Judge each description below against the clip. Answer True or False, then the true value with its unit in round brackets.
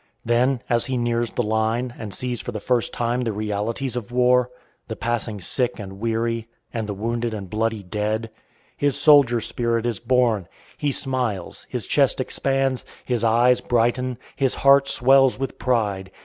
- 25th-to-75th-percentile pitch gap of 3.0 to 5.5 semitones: False (2.4 semitones)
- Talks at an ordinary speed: True (165 wpm)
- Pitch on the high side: False (120 Hz)